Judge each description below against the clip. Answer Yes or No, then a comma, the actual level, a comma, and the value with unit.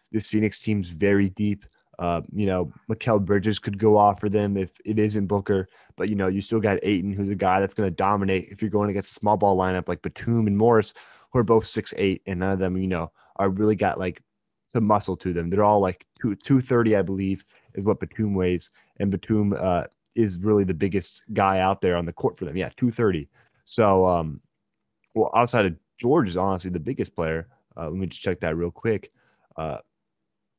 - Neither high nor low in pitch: No, low, 100 Hz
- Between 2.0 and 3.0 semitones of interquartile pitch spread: Yes, narrow, 2.4 semitones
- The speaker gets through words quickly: Yes, fast, 225 wpm